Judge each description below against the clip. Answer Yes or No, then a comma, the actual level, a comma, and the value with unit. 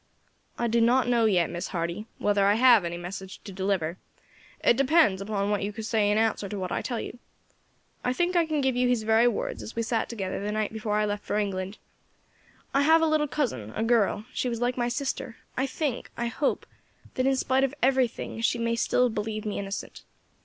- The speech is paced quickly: Yes, fast, 220 wpm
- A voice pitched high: Yes, high, 225 Hz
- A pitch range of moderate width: Yes, average, 3.7 semitones